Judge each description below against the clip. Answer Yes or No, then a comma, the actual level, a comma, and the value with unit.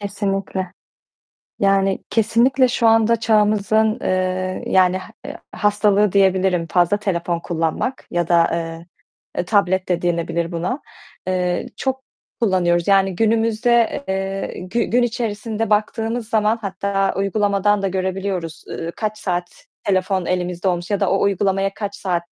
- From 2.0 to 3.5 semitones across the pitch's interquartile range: Yes, average, 2.9 semitones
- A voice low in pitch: No, high, 195 Hz